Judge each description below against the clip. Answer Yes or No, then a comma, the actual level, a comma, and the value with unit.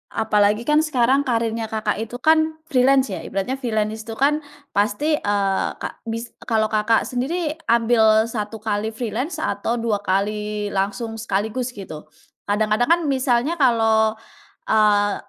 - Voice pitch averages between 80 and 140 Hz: No, high, 225 Hz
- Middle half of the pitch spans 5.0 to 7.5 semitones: No, average, 3.3 semitones